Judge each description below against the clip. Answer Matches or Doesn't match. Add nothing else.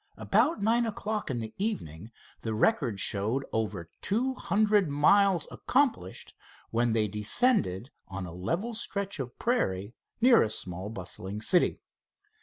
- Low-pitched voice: Matches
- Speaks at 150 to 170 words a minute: Doesn't match